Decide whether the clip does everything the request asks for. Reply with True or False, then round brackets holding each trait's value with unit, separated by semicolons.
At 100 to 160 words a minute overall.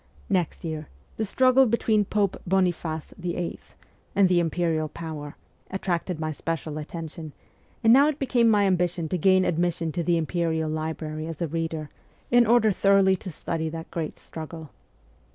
True (155 wpm)